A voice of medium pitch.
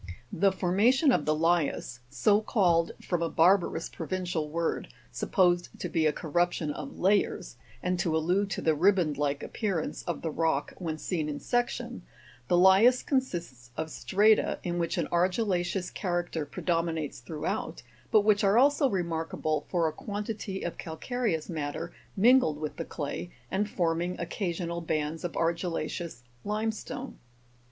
Yes: medium, 175 Hz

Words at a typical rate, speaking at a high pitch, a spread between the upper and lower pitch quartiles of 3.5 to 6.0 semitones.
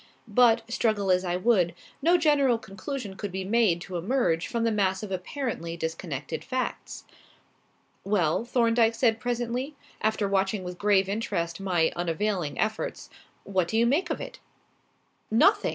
Yes: average, 150 wpm; high, 210 Hz; average, 4.5 semitones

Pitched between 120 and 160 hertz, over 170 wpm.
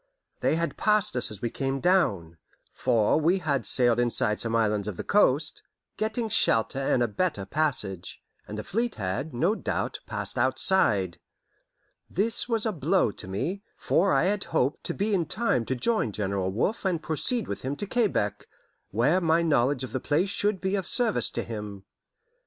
Yes: medium, 140 Hz; average, 180 wpm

